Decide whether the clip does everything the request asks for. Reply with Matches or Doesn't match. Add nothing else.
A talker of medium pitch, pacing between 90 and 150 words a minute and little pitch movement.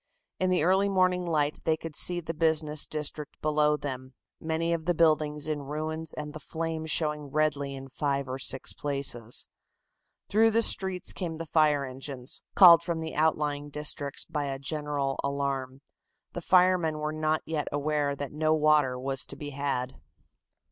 Doesn't match